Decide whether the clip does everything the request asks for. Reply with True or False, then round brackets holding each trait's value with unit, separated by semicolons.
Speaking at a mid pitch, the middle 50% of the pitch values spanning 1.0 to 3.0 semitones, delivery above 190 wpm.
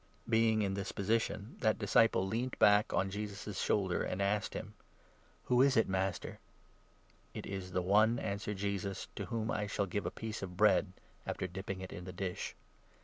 False (100 Hz; 2.4 semitones; 200 wpm)